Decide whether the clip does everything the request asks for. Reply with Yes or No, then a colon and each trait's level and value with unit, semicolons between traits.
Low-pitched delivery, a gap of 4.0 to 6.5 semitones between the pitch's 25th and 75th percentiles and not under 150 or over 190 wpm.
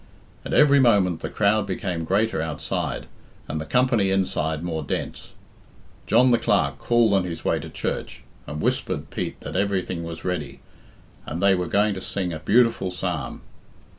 Yes: very low, 95 Hz; average, 4.3 semitones; average, 165 wpm